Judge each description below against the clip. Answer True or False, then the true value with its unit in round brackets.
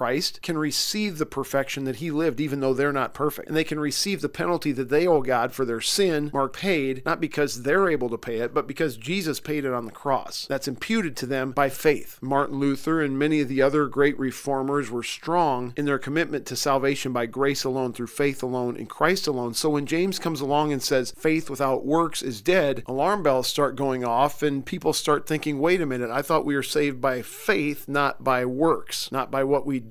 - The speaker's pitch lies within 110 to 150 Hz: True (140 Hz)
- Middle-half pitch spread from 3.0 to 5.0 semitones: False (2.6 semitones)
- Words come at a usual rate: False (225 wpm)